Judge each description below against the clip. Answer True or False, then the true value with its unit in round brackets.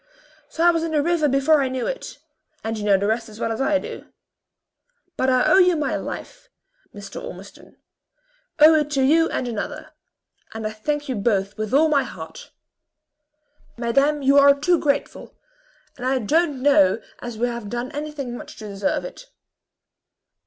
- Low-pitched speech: False (270 Hz)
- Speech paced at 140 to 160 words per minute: False (180 wpm)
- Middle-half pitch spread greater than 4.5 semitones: True (5.2 semitones)